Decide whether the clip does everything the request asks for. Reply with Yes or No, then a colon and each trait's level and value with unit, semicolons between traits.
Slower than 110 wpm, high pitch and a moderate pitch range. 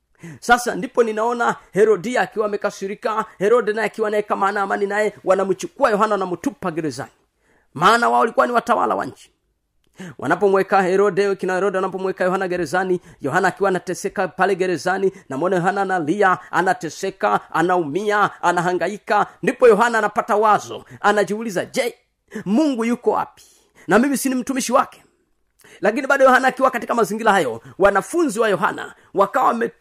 No: average, 115 wpm; high, 200 Hz; average, 3.4 semitones